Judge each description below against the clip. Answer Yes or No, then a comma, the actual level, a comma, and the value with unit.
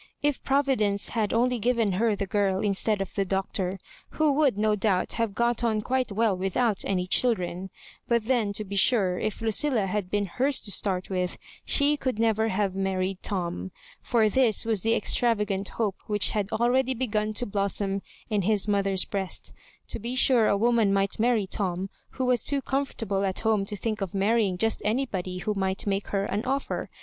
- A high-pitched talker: Yes, high, 210 Hz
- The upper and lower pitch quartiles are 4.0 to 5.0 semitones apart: No, average, 3.2 semitones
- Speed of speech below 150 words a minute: No, average, 190 wpm